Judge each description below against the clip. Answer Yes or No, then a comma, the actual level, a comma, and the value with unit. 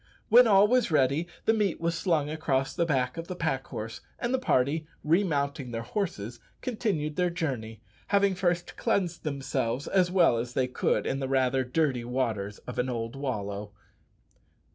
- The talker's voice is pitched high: No, medium, 145 Hz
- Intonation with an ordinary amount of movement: No, wide, 5.9 semitones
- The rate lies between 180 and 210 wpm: No, average, 170 wpm